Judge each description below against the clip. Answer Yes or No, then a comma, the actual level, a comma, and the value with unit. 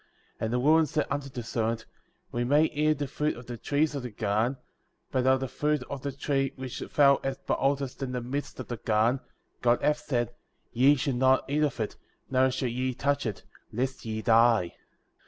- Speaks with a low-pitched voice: Yes, low, 130 Hz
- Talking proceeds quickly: Yes, fast, 220 wpm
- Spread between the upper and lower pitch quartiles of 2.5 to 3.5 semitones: Yes, average, 2.9 semitones